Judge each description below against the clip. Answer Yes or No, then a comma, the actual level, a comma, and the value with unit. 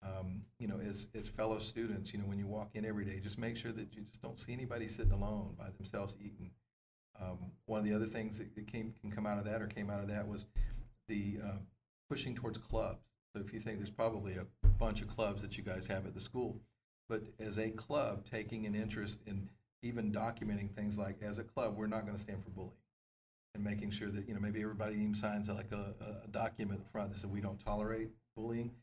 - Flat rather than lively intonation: Yes, narrow, 1.6 semitones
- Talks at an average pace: No, fast, 235 wpm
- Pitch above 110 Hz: No, low, 105 Hz